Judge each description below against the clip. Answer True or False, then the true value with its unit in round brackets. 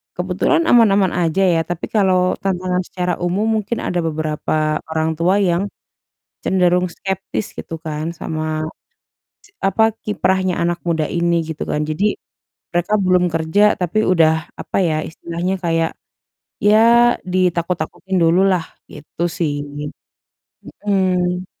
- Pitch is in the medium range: True (180 Hz)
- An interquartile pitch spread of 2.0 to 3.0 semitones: True (2.5 semitones)